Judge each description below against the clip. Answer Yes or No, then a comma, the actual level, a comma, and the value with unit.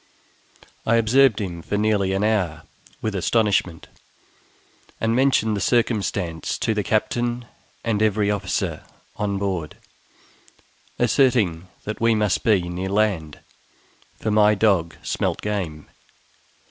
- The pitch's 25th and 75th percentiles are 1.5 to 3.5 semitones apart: Yes, average, 2.9 semitones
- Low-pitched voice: Yes, low, 105 Hz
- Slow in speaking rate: Yes, slow, 120 wpm